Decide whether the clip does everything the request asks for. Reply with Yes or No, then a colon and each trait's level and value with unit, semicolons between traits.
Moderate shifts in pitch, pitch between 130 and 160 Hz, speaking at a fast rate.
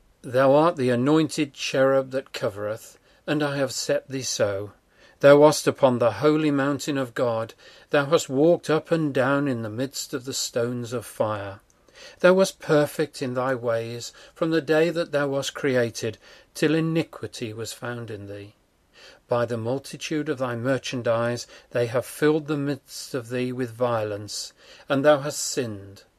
No: average, 4.0 semitones; low, 135 Hz; average, 165 wpm